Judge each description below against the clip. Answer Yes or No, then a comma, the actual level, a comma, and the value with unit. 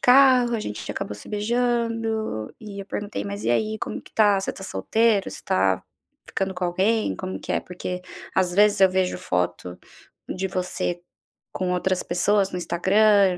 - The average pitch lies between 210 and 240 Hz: No, high, 190 Hz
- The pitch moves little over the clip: No, average, 3.2 semitones